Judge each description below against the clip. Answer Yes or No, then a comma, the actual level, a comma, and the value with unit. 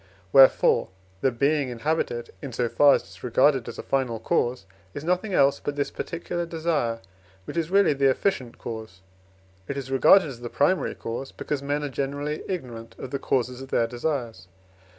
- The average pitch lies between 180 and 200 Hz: No, low, 135 Hz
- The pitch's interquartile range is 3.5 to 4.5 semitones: Yes, average, 3.8 semitones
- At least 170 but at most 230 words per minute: Yes, average, 185 wpm